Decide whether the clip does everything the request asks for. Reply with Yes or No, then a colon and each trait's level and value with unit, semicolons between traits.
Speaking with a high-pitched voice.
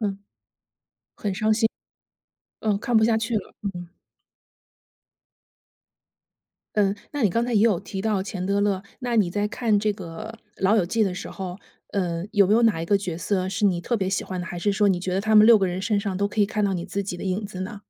Yes: high, 200 Hz